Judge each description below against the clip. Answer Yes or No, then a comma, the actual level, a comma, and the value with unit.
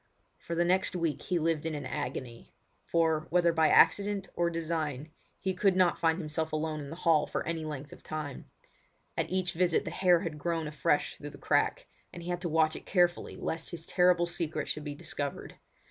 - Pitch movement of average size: No, narrow, 2.3 semitones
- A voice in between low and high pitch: Yes, medium, 165 Hz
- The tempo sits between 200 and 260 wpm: Yes, fast, 205 wpm